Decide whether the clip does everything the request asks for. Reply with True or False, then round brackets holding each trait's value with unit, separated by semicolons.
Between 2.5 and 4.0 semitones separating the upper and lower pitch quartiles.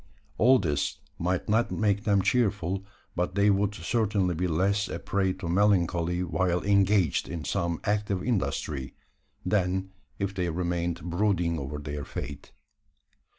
True (2.9 semitones)